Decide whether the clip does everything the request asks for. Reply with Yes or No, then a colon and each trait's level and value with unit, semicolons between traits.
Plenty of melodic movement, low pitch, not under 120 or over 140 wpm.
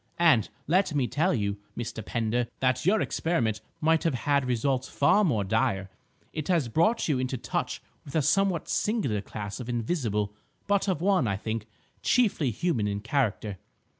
No: wide, 7.1 semitones; low, 130 Hz; average, 165 wpm